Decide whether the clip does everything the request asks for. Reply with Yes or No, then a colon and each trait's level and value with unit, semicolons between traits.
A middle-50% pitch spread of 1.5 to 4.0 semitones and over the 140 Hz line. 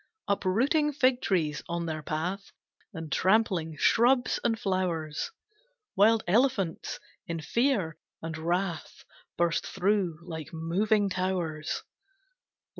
No: average, 4.9 semitones; medium, 185 Hz